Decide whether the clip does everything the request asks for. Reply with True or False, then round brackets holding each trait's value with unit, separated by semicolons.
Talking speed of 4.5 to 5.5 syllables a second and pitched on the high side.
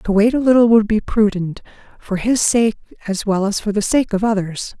True (5.2 syllables/s; 215 Hz)